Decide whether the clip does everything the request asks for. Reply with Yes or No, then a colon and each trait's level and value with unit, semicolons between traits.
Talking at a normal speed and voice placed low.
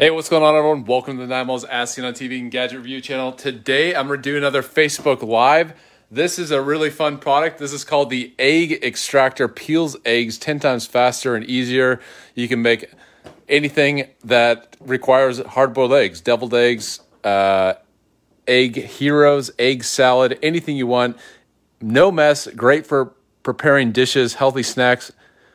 Yes: average, 160 wpm; low, 130 Hz